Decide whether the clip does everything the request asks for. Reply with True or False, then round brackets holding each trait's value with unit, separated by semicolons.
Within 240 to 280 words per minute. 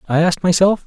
False (210 wpm)